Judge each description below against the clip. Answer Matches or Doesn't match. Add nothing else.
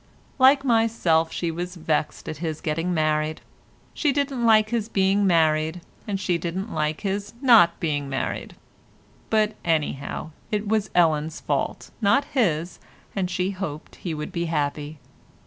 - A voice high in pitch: Doesn't match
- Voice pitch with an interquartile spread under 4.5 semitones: Doesn't match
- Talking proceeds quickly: Doesn't match